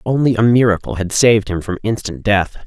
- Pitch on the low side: Yes, low, 105 Hz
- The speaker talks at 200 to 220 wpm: Yes, fast, 205 wpm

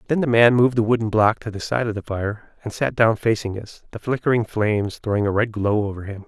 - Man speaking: Yes, male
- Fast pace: Yes, fast, 260 wpm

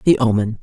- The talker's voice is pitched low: Yes, low, 115 Hz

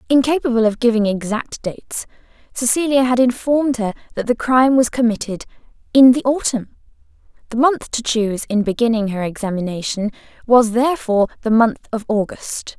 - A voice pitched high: Yes, high, 235 Hz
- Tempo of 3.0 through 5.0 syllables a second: No, 5.6 syllables/s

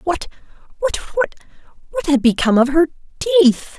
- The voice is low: No, very high, 255 Hz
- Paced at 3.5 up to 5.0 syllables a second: No, 5.5 syllables/s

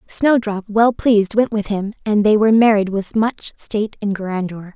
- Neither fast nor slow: Yes, average, 190 wpm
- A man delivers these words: No, female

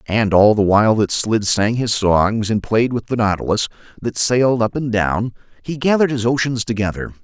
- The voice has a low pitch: Yes, low, 110 Hz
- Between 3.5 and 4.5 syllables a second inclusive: No, 5.2 syllables/s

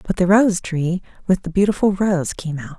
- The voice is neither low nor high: Yes, medium, 180 Hz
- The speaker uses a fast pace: Yes, fast, 215 wpm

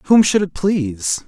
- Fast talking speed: No, average, 190 wpm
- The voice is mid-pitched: Yes, medium, 170 Hz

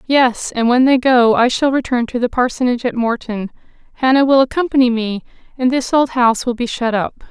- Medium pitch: No, high, 245 Hz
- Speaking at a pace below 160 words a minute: No, fast, 205 wpm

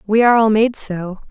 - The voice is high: Yes, high, 215 Hz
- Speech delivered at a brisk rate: Yes, fast, 230 wpm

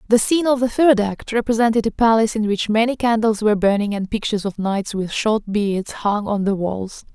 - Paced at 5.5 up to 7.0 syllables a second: Yes, 5.6 syllables/s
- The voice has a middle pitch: No, high, 215 Hz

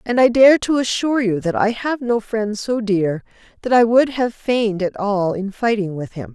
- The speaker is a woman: Yes, female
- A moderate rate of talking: No, fast, 225 wpm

